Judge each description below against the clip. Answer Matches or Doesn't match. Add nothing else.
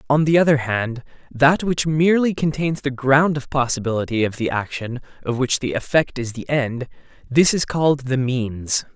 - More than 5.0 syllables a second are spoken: Doesn't match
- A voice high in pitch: Doesn't match